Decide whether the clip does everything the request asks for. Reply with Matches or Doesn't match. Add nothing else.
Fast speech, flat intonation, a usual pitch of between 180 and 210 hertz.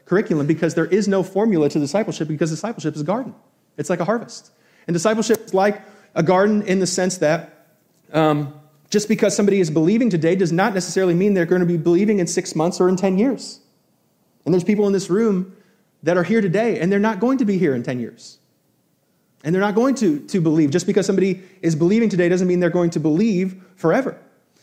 Doesn't match